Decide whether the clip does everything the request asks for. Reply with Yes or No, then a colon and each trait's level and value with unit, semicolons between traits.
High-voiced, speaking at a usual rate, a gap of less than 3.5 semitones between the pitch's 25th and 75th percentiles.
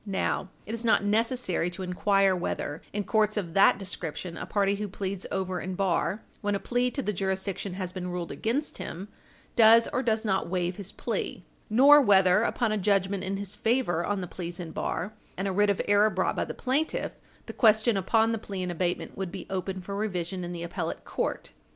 No: high, 195 Hz; fast, 210 wpm; average, 2.8 semitones